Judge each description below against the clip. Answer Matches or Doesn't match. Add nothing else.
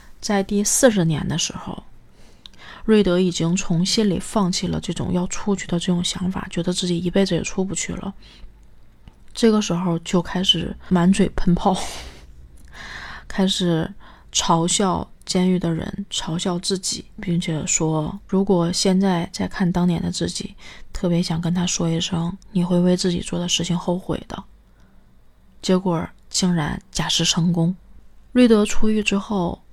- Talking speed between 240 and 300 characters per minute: Doesn't match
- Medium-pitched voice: Matches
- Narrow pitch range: Matches